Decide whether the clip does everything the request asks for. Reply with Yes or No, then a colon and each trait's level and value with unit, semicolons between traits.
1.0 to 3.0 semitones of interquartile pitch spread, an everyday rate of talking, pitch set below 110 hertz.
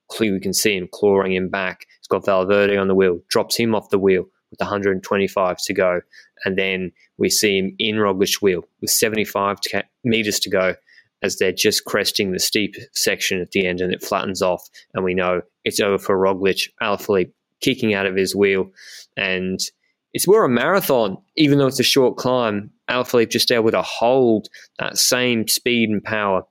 Yes: average, 2.7 semitones; average, 190 wpm; low, 100 Hz